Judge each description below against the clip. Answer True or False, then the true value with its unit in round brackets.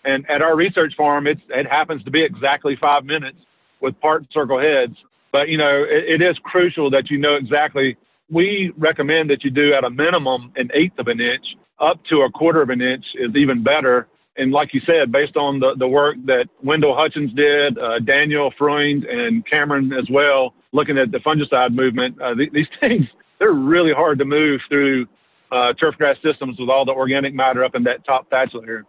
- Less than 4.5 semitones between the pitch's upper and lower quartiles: True (2.6 semitones)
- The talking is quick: True (210 wpm)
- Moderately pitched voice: True (145 Hz)